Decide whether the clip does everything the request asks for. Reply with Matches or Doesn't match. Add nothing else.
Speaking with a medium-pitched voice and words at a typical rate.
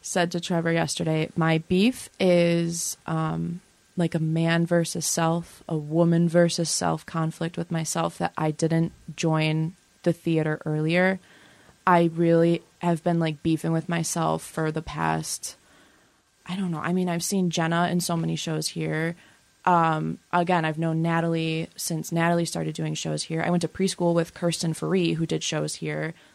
Matches